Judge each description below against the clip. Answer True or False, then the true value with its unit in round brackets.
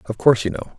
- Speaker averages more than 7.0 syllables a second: True (7.6 syllables/s)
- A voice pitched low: True (105 Hz)